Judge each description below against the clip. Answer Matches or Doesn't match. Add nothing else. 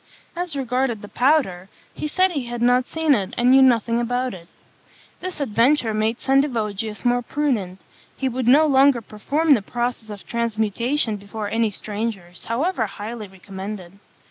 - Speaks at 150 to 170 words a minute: Matches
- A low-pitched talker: Doesn't match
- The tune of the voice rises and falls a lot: Doesn't match